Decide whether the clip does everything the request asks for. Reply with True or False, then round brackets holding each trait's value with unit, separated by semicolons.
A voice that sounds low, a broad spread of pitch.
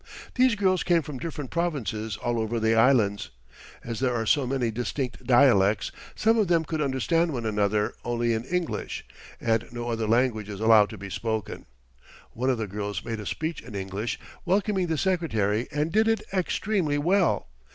True (120 Hz; 7.0 semitones)